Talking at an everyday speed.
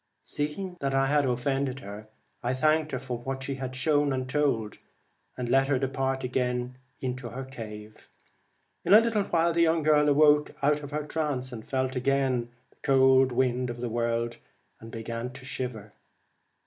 Yes: average, 175 wpm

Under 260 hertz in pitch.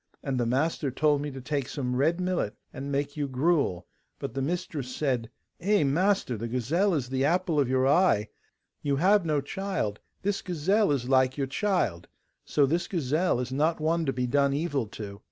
Yes: medium, 140 Hz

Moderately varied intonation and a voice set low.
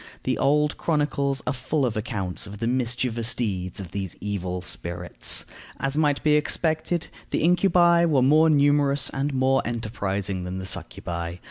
No: wide, 7.0 semitones; low, 130 Hz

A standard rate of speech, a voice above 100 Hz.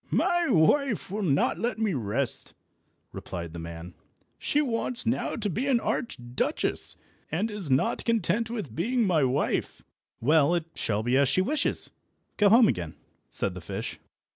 Yes: average, 160 wpm; medium, 185 Hz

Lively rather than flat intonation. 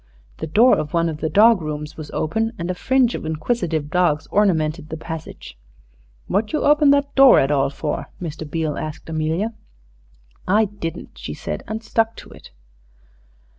Yes: wide, 6.2 semitones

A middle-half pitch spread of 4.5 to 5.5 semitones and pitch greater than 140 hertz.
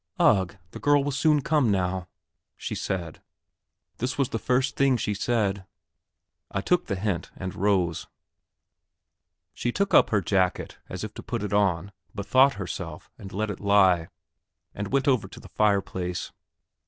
No: average, 5.2 semitones; low, 100 Hz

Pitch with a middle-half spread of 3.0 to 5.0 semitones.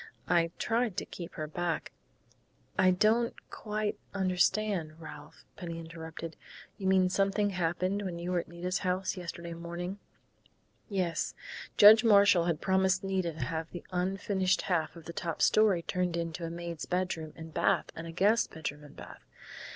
No: narrow, 2.5 semitones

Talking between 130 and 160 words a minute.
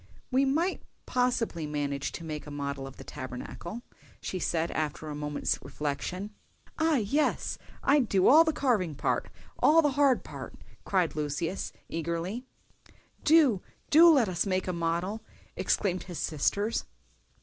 Yes: average, 140 wpm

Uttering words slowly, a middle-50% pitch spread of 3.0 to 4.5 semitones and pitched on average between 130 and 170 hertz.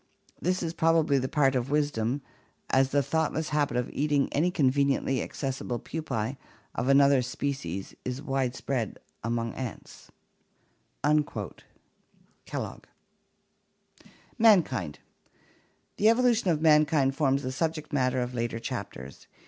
Yes: slow, 115 wpm; average, 3.4 semitones; medium, 140 Hz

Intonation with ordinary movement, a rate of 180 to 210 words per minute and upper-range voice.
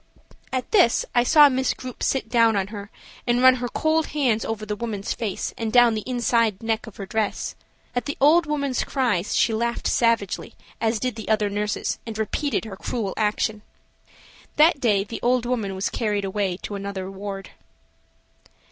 Yes: average, 3.4 semitones; average, 185 wpm; high, 225 Hz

